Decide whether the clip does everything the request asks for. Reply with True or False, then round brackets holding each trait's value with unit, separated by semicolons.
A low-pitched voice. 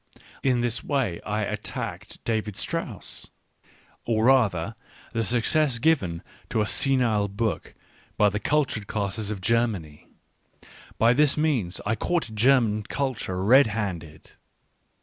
True (110 Hz)